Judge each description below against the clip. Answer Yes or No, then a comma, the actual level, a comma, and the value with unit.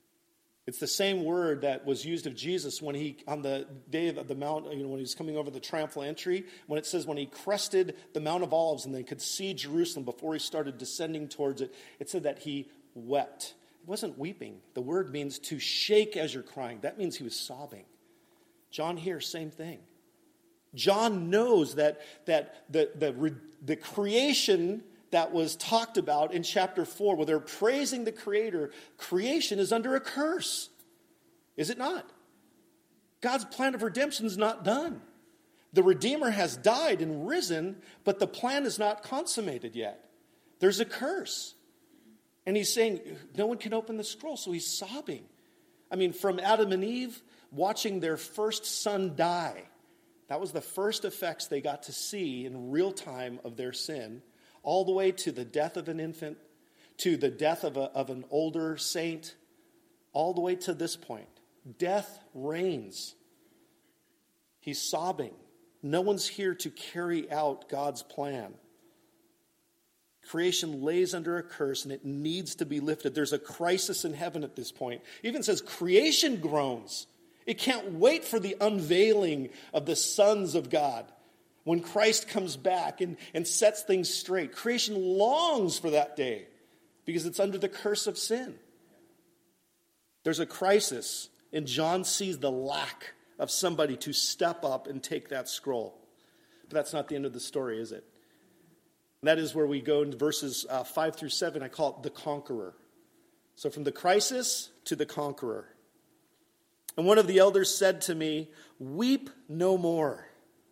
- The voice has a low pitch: No, medium, 180 Hz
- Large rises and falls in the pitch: Yes, wide, 7.0 semitones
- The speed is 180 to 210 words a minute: No, average, 170 wpm